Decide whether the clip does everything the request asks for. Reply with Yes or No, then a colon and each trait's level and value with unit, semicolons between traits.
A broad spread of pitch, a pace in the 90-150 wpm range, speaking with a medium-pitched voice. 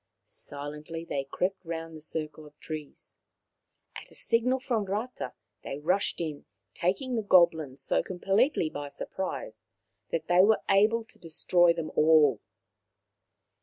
No: average, 4.5 semitones; slow, 135 wpm; medium, 170 Hz